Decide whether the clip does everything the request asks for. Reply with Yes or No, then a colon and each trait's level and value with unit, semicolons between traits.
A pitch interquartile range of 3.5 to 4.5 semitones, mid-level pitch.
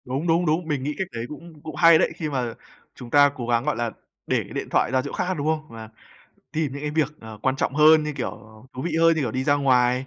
Yes: average, 3.8 semitones; medium, 145 Hz